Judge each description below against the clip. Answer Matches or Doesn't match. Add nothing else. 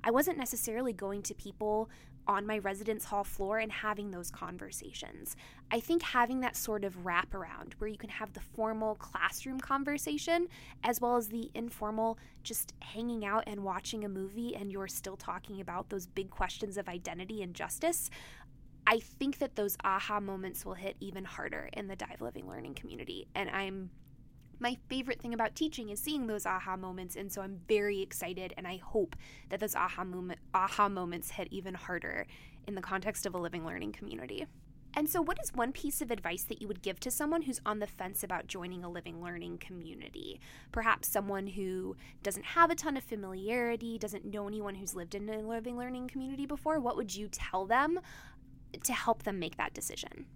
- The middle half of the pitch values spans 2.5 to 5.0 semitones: Matches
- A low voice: Doesn't match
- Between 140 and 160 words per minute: Doesn't match